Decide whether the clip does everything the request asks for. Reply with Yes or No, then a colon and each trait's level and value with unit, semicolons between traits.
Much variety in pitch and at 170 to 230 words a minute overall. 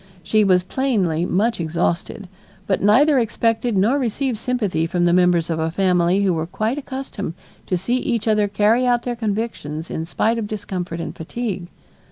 No: average, 5.0 semitones; average, 175 wpm